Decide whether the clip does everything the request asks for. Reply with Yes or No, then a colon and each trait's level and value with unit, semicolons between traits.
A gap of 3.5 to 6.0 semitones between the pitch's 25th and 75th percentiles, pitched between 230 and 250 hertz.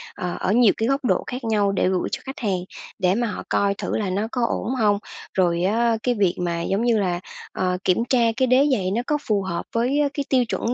No: average, 4.6 semitones; high, 215 Hz